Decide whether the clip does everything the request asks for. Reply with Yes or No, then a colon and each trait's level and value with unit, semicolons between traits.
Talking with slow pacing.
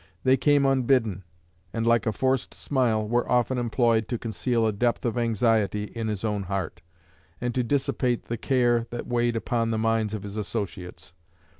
No: average, 175 wpm